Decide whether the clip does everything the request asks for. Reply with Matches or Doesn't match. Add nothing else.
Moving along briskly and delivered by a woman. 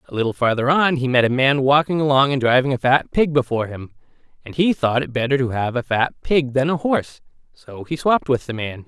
Doesn't match